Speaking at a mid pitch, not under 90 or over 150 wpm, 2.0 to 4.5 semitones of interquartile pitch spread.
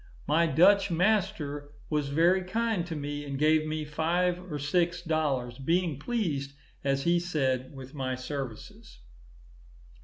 Yes: medium, 155 Hz; slow, 135 wpm; average, 4.1 semitones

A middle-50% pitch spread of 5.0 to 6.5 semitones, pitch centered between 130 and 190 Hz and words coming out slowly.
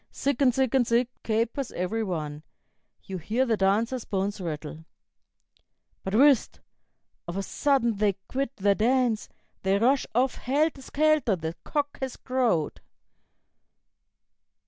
No: average, 5.3 semitones; high, 230 Hz; slow, 130 wpm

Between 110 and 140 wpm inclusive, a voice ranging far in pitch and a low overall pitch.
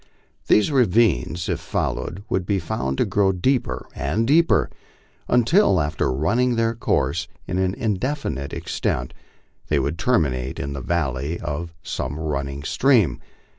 Yes: slow, 135 wpm; wide, 8.2 semitones; very low, 90 Hz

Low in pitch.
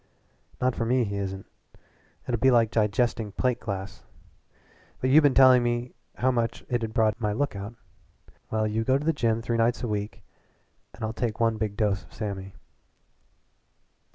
Yes: low, 115 Hz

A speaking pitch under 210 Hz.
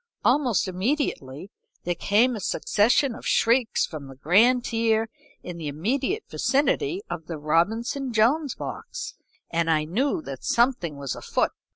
No: high, 220 Hz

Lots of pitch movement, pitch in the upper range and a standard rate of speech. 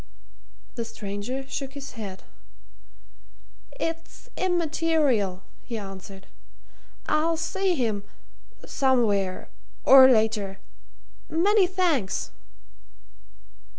No: wide, 8.2 semitones; very high, 260 Hz; slow, 75 wpm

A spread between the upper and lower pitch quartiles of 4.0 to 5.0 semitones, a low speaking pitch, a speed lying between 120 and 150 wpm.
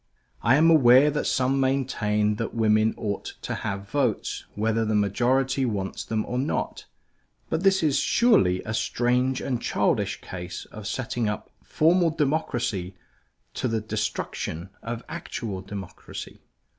Yes: average, 4.4 semitones; low, 115 Hz; average, 140 wpm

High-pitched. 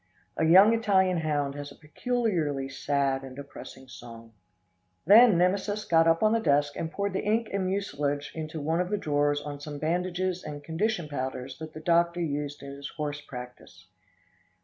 No: medium, 155 Hz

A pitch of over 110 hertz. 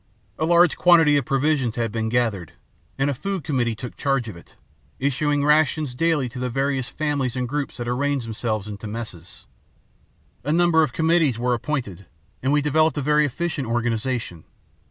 Yes: low, 135 Hz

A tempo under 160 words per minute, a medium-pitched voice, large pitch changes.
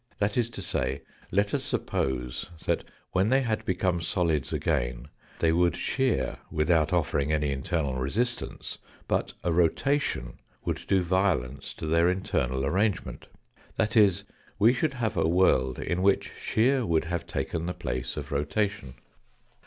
No: average, 150 wpm; very low, 85 Hz; wide, 6.2 semitones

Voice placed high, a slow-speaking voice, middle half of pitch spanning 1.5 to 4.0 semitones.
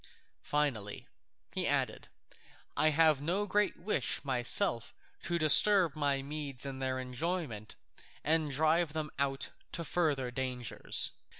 No: medium, 145 Hz; slow, 120 wpm; average, 3.7 semitones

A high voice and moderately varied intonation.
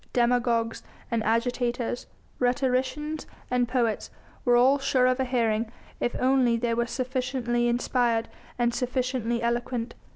No: high, 245 Hz; narrow, 1.3 semitones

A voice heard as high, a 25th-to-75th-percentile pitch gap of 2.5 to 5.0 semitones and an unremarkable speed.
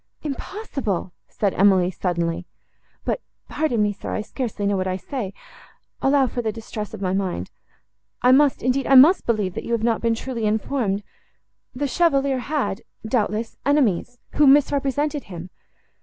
No: high, 230 Hz; wide, 5.6 semitones; average, 155 wpm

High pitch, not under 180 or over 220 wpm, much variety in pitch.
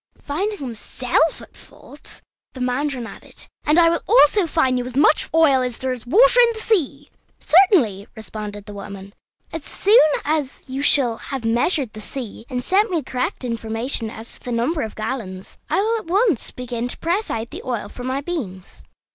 Yes: very high, 260 Hz; average, 185 wpm; wide, 6.0 semitones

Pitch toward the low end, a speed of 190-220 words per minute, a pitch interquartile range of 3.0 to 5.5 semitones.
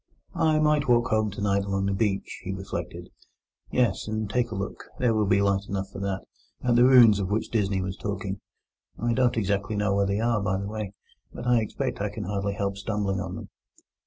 No: low, 100 Hz; average, 200 wpm; narrow, 2.6 semitones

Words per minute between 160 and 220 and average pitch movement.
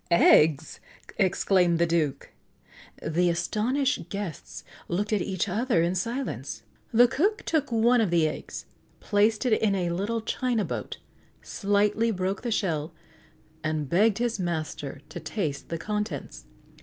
No: average, 140 wpm; average, 4.9 semitones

